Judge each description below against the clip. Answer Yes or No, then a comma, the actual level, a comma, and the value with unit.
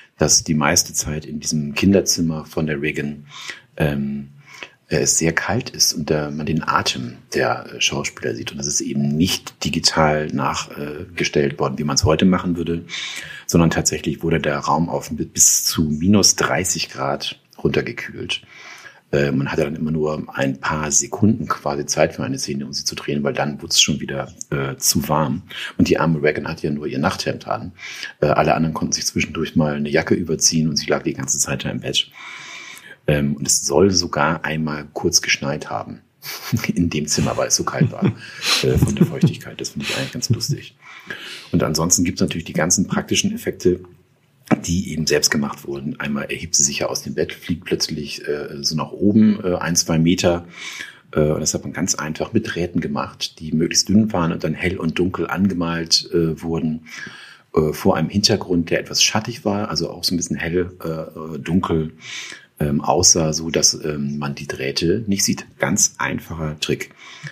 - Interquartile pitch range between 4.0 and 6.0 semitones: No, average, 2.7 semitones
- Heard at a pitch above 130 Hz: No, very low, 80 Hz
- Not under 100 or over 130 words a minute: No, fast, 190 wpm